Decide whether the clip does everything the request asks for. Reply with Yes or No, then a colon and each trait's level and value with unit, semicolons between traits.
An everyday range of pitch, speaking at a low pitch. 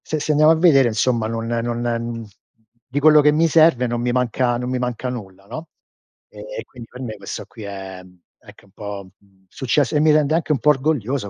Yes: average, 5.0 semitones; low, 125 Hz